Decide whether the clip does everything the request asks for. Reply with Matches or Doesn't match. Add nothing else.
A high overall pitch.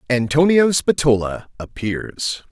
Doesn't match